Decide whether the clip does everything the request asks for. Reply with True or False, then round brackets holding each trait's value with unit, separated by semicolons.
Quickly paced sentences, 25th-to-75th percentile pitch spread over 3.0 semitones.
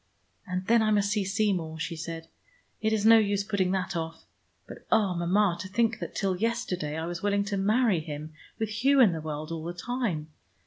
True (210 wpm; 4.5 semitones)